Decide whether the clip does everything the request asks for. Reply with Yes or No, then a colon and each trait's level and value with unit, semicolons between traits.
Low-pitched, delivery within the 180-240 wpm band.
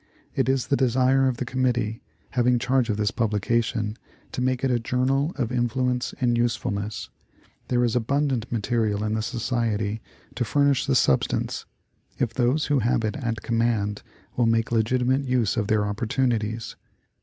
No: low, 120 Hz; average, 160 wpm